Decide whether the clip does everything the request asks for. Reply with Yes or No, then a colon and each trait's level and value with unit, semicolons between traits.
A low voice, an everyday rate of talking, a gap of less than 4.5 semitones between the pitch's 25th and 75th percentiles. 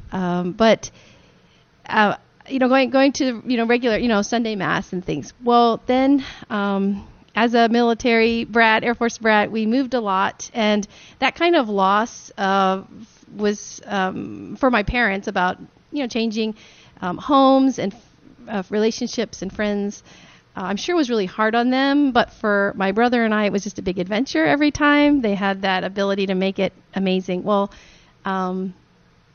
No: high, 220 Hz; average, 180 wpm; average, 3.5 semitones